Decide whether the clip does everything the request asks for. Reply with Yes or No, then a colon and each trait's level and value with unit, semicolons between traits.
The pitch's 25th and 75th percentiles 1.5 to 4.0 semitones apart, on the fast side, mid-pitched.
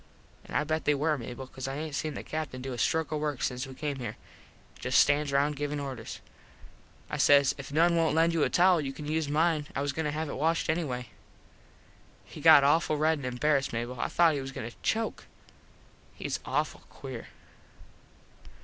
Yes: average, 2.8 semitones; fast, 210 wpm; medium, 145 Hz